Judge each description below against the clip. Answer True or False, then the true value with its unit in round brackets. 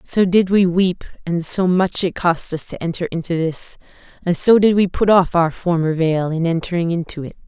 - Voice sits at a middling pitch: True (175 Hz)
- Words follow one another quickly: True (215 wpm)